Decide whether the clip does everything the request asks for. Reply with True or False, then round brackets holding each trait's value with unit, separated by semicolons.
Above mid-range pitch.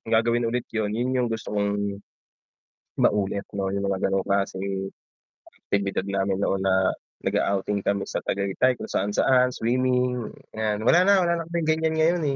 False (105 Hz)